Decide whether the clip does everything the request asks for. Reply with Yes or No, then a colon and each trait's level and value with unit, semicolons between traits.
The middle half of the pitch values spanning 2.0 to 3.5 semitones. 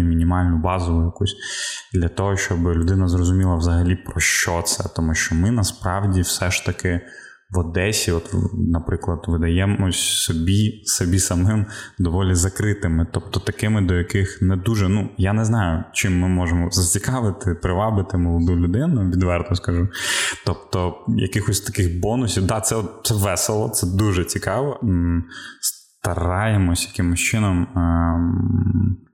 Yes: average, 3.1 semitones